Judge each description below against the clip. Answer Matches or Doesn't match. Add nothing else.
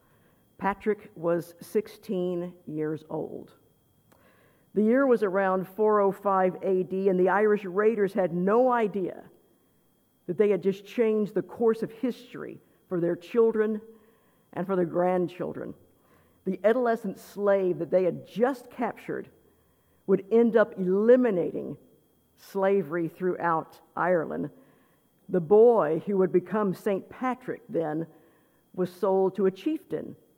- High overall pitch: Matches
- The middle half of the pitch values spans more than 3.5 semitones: Doesn't match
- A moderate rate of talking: Doesn't match